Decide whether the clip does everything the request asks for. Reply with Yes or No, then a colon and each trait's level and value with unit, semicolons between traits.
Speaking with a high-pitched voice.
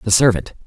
No: low, 110 Hz